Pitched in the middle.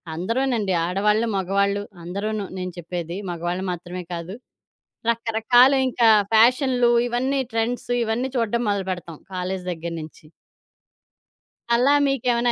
No: high, 210 Hz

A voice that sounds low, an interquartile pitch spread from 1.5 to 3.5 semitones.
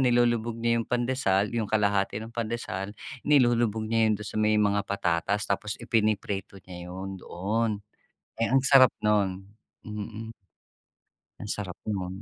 Yes: low, 105 Hz; average, 2.8 semitones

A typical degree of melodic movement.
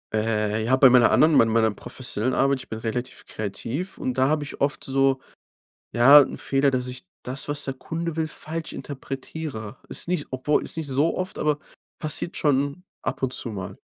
Yes: average, 3.6 semitones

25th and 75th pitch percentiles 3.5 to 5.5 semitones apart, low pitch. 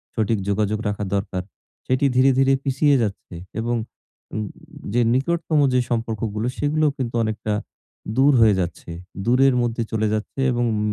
Yes: average, 3.9 semitones; low, 120 Hz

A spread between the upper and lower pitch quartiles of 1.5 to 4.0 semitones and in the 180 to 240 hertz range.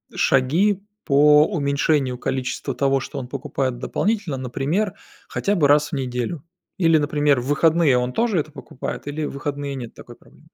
No: average, 3.0 semitones; medium, 145 Hz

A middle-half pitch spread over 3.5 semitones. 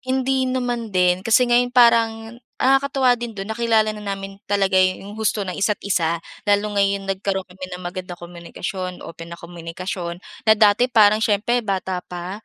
Yes: average, 4.0 semitones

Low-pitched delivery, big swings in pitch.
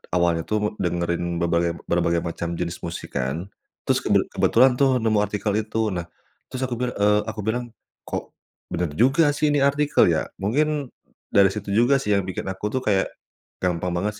Yes: low, 100 Hz; wide, 5.7 semitones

